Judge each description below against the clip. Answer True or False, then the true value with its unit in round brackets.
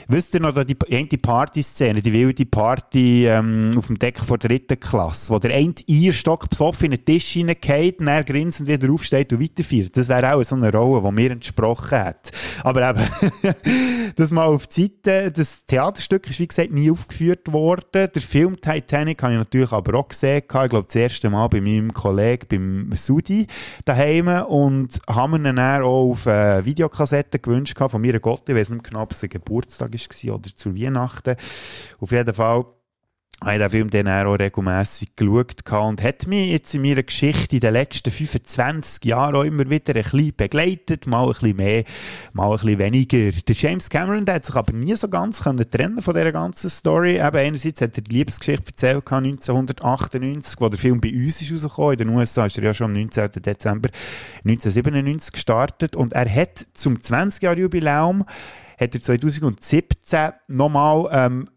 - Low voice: True (130 Hz)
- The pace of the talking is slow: False (180 wpm)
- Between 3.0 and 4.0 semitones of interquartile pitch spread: False (5.0 semitones)